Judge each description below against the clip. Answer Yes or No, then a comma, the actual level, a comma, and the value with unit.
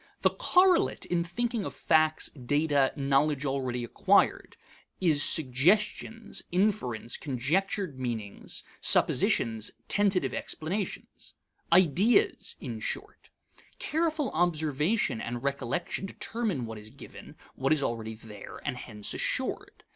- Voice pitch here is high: No, medium, 150 Hz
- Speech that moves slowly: Yes, slow, 110 wpm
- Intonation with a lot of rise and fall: Yes, wide, 7.6 semitones